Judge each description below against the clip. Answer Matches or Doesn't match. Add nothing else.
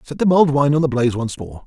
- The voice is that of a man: Matches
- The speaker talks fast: Matches